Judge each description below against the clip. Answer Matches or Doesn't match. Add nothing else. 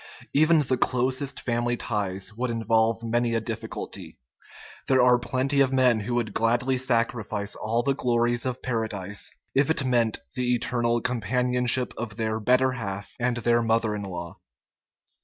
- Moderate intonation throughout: Doesn't match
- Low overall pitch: Matches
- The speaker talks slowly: Doesn't match